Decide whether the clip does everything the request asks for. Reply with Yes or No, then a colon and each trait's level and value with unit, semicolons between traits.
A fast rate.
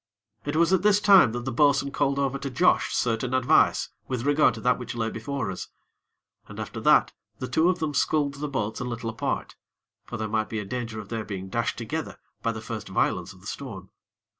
Yes: fast, 220 wpm